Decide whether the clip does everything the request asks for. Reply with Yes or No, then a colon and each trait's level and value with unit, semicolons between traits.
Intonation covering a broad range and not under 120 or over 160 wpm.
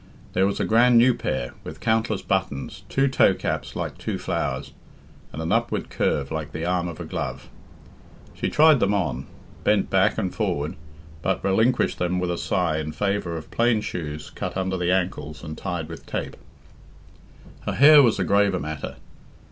No: wide, 5.8 semitones; average, 175 wpm